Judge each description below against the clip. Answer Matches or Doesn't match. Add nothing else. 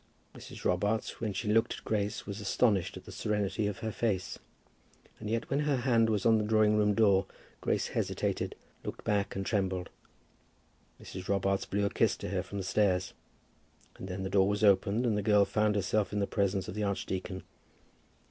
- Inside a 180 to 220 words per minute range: Matches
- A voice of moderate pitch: Doesn't match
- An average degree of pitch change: Doesn't match